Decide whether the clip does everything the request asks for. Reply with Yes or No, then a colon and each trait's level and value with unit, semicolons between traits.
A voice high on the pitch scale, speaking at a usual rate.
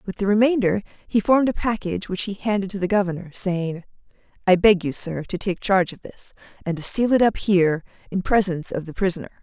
No: high, 195 Hz; fast, 215 wpm